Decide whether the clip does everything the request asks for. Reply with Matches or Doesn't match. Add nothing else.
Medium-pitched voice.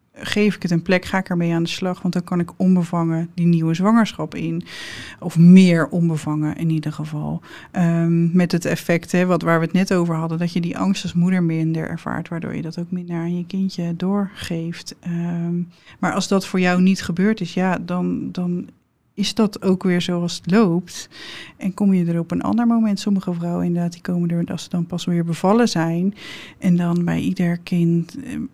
Matches